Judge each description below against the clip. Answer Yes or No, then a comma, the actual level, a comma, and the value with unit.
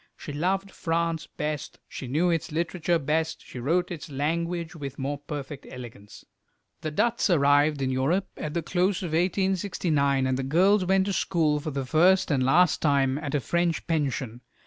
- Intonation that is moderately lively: Yes, average, 3.9 semitones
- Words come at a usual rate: Yes, average, 175 wpm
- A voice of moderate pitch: Yes, medium, 155 Hz